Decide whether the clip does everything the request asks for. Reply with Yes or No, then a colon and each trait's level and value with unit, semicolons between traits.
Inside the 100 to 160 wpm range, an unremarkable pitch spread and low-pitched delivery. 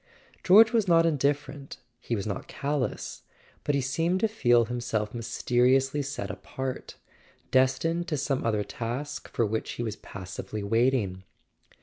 Yes: average, 145 wpm; average, 4.1 semitones; low, 130 Hz